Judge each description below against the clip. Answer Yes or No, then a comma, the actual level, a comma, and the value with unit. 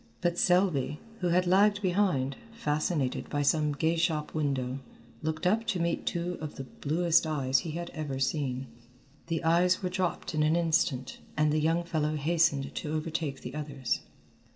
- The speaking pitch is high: No, medium, 155 Hz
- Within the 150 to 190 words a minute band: Yes, average, 170 wpm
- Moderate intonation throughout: Yes, average, 3.1 semitones